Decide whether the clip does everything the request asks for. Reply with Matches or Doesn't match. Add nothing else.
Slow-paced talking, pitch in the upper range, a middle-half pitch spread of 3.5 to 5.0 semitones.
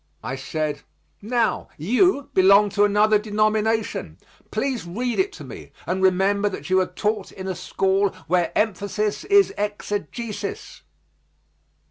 Doesn't match